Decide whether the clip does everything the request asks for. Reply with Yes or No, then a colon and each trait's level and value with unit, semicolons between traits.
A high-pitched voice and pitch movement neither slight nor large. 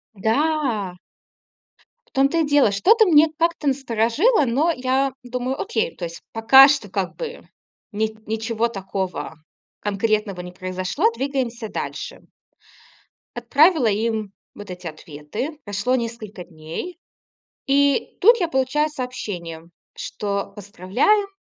No: high, 235 Hz; wide, 6.4 semitones